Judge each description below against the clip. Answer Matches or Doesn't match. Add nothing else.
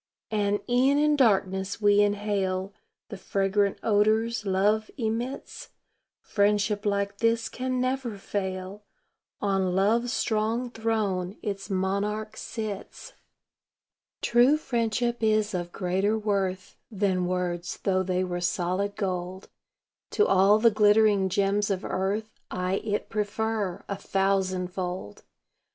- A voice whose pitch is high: Matches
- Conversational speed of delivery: Doesn't match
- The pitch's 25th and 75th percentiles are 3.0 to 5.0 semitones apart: Doesn't match